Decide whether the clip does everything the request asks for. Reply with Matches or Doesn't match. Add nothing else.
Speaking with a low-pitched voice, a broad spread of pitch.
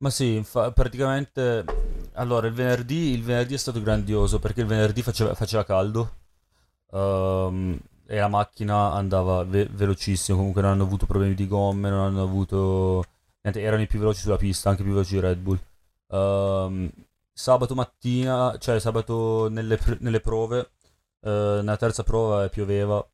Doesn't match